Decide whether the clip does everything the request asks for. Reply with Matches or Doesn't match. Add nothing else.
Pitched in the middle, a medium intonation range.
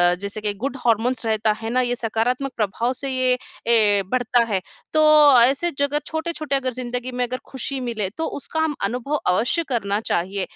Doesn't match